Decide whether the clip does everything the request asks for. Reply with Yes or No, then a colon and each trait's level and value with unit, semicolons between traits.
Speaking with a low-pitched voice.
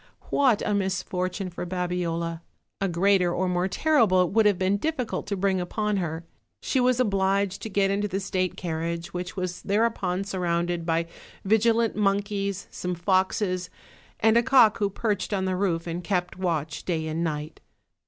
No: high, 190 Hz